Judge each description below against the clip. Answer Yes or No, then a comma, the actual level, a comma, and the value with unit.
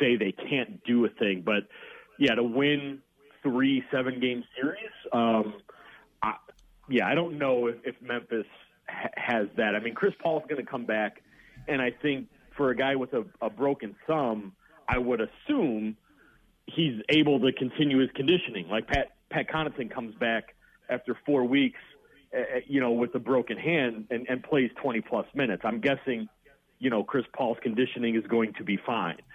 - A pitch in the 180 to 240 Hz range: No, low, 130 Hz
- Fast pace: No, average, 180 wpm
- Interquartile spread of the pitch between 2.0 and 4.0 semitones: Yes, average, 3.2 semitones